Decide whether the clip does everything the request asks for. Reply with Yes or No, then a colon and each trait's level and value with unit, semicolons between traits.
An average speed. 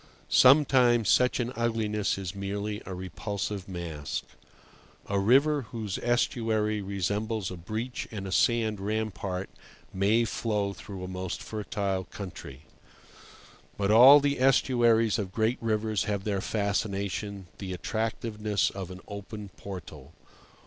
No: slow, 125 wpm